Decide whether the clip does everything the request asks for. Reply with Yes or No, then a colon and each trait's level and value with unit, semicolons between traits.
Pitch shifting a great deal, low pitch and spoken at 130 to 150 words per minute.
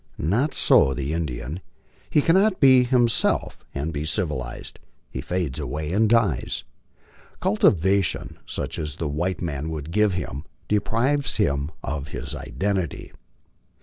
Yes: wide, 6.7 semitones; very low, 85 Hz; slow, 135 wpm